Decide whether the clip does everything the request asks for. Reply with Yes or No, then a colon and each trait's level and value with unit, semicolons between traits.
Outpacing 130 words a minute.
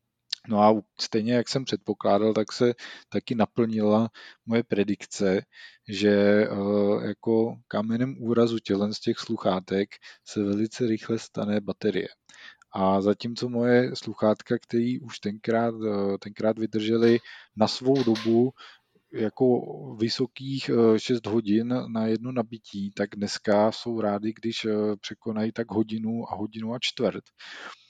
No: average, 120 wpm